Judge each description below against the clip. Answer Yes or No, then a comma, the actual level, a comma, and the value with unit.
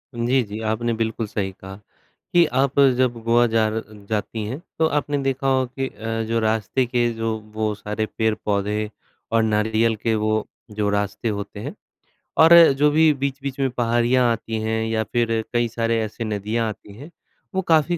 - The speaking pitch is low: Yes, low, 115 Hz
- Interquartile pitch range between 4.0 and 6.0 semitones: No, average, 2.7 semitones